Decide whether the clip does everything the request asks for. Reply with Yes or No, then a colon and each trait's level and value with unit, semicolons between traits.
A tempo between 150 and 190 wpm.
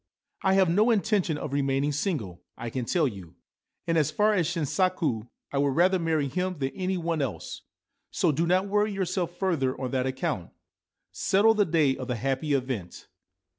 Yes: average, 185 wpm